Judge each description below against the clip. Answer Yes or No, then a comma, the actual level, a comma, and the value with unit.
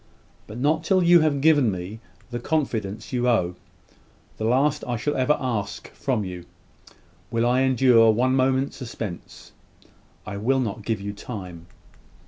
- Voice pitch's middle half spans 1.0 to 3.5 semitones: No, average, 4.2 semitones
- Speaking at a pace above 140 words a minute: Yes, average, 150 wpm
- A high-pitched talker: No, low, 120 Hz